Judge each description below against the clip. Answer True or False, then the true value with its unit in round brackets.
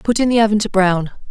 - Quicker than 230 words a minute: True (275 wpm)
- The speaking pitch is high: True (205 Hz)